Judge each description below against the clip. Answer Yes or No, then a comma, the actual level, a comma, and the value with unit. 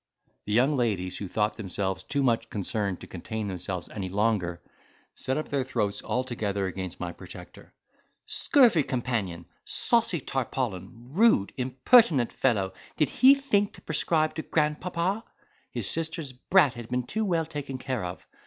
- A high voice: No, low, 125 Hz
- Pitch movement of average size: No, wide, 7.4 semitones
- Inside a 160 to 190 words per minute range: No, average, 145 wpm